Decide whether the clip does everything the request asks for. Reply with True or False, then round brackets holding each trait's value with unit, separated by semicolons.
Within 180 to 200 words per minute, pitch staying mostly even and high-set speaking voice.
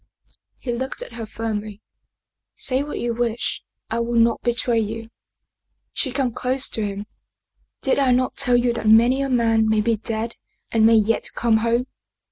True (185 wpm; 2.0 semitones; 235 Hz)